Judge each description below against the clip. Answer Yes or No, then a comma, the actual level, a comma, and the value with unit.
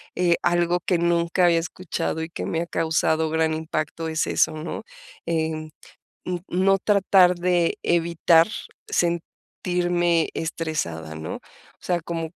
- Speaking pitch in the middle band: Yes, medium, 170 Hz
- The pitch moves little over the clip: Yes, narrow, 1.6 semitones